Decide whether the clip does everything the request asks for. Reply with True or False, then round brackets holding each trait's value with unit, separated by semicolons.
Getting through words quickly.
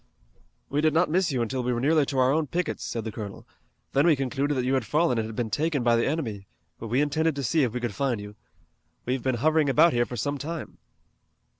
True (250 wpm)